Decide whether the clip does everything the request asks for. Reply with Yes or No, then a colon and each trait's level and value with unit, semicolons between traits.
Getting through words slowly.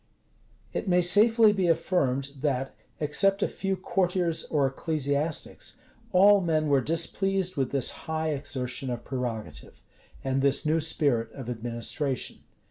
Yes: slow, 130 wpm